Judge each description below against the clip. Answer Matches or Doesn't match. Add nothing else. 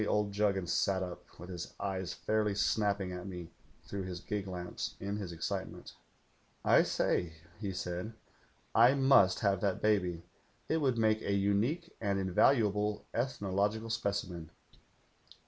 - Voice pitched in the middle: Doesn't match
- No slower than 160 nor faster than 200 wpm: Doesn't match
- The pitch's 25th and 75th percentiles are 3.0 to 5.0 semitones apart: Doesn't match